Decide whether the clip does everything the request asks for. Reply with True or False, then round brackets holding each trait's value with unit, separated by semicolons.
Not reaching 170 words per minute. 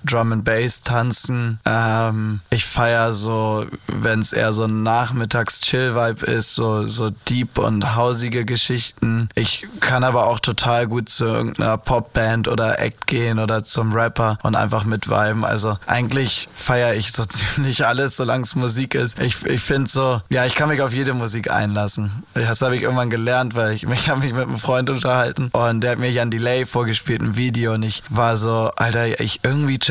False (190 wpm)